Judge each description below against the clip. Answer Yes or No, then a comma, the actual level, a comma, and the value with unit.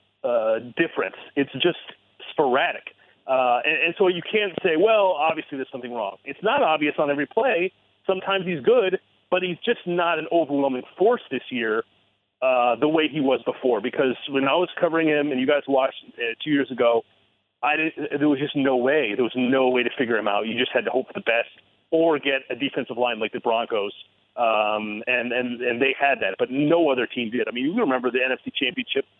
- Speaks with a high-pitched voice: No, medium, 140 Hz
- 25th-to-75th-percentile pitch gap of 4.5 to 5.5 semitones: Yes, average, 4.9 semitones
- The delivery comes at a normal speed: No, fast, 215 wpm